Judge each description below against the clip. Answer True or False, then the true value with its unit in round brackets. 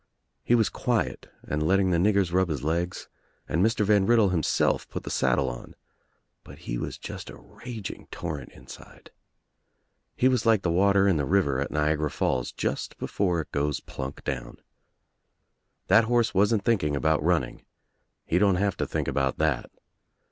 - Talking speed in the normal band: True (170 wpm)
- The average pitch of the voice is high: False (90 Hz)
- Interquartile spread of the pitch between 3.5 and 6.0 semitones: True (5.3 semitones)